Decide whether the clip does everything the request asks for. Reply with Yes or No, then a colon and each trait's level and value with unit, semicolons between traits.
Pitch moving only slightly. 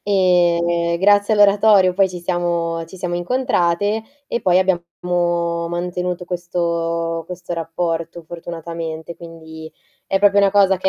Yes: narrow, 2.1 semitones